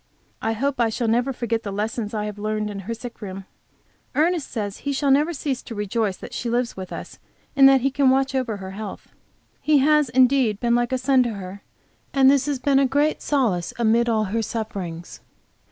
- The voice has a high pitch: Yes, high, 235 Hz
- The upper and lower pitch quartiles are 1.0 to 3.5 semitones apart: No, average, 4.2 semitones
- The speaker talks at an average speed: No, fast, 215 wpm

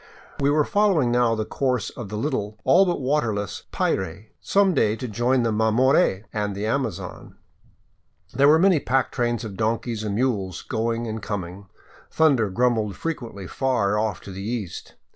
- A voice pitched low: Yes, low, 115 Hz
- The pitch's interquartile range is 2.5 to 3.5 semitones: No, average, 4.3 semitones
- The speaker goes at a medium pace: Yes, average, 165 wpm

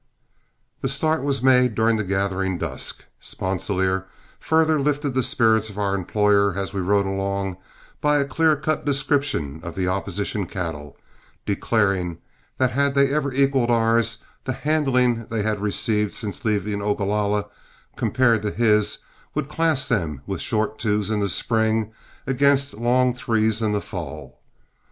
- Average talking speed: Yes, average, 150 wpm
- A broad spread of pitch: No, average, 4.9 semitones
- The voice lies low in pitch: Yes, low, 110 Hz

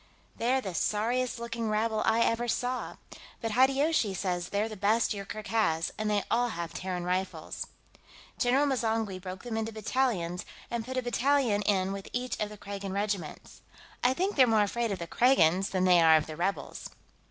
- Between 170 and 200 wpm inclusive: Yes, average, 185 wpm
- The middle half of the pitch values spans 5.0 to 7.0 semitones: No, average, 4.1 semitones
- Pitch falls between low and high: No, high, 215 Hz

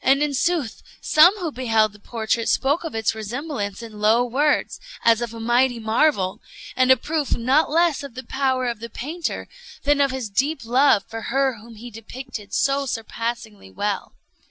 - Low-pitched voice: No, high, 245 Hz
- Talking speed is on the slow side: No, average, 180 wpm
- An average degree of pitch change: Yes, average, 3.8 semitones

